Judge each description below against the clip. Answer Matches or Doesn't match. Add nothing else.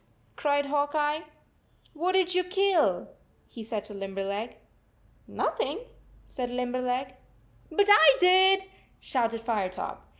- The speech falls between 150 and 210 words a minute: Doesn't match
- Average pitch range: Doesn't match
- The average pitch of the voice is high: Matches